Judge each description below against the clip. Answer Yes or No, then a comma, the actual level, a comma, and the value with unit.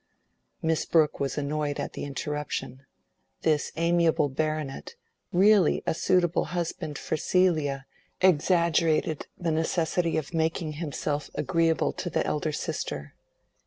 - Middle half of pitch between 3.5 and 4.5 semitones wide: No, narrow, 2.4 semitones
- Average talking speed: No, slow, 120 wpm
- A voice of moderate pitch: Yes, medium, 160 Hz